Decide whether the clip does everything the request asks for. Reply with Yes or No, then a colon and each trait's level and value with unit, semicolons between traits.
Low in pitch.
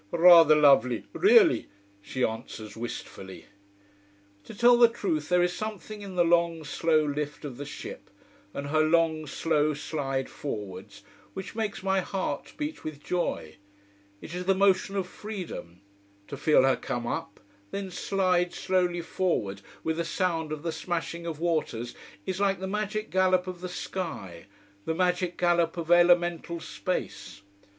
No: medium, 170 Hz